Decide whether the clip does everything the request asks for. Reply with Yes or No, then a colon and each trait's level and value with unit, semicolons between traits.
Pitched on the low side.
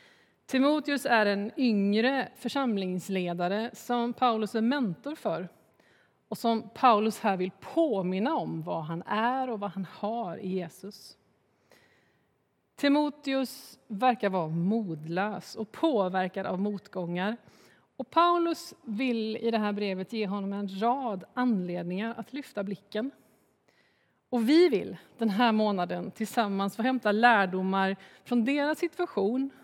No: high, 220 Hz